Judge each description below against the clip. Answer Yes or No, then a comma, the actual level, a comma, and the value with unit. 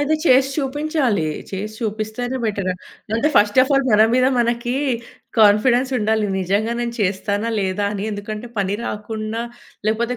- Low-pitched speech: No, high, 220 Hz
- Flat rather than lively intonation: No, average, 3.2 semitones